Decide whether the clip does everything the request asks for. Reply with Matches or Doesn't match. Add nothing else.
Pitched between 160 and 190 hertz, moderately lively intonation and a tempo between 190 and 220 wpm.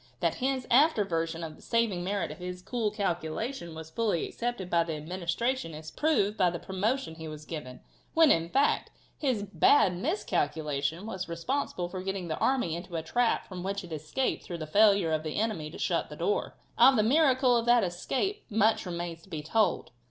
Doesn't match